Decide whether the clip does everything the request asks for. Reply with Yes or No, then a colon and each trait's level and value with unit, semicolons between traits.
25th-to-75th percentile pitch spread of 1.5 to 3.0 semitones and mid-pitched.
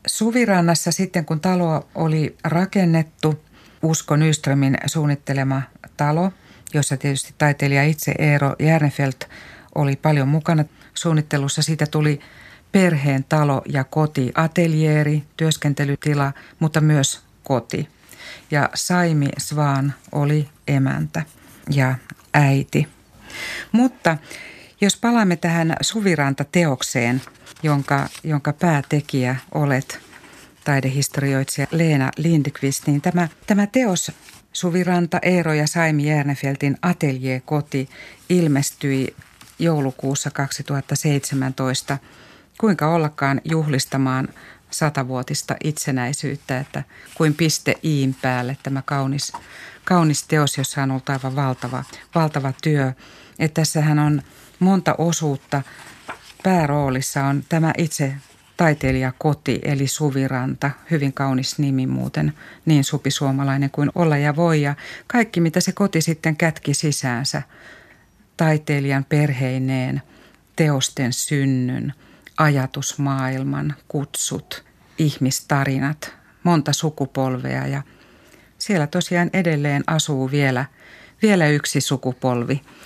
Yes: average, 2.7 semitones; medium, 145 Hz